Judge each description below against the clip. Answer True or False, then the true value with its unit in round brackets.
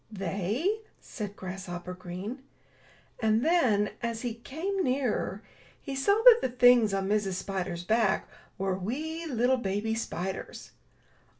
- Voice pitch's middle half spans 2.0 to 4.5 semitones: False (5.3 semitones)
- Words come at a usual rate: False (125 wpm)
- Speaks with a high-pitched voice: True (220 Hz)